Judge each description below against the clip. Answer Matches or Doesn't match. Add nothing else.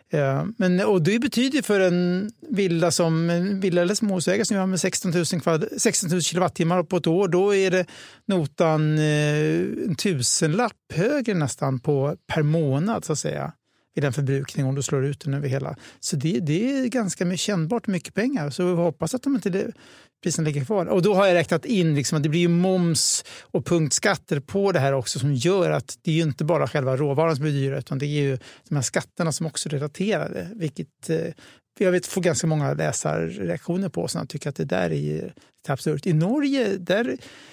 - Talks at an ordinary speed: Doesn't match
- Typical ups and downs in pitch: Matches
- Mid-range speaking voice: Matches